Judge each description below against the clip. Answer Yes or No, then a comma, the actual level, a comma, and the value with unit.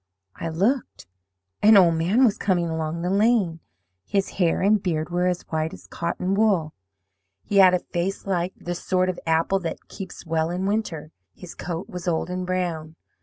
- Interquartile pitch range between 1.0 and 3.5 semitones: Yes, average, 2.8 semitones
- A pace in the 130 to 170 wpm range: No, average, 180 wpm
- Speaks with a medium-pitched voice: Yes, medium, 180 Hz